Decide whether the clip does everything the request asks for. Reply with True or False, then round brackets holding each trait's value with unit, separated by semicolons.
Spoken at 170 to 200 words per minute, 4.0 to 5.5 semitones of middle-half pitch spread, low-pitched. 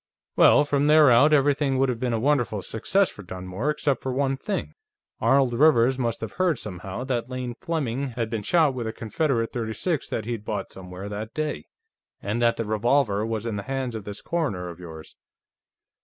True (195 wpm; 4.7 semitones; 120 Hz)